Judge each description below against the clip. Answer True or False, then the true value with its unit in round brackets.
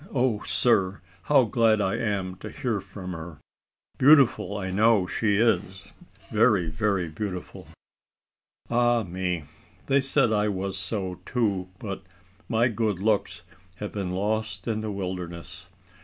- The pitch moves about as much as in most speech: True (3.2 semitones)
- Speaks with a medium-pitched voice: False (105 Hz)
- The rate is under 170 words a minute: True (135 wpm)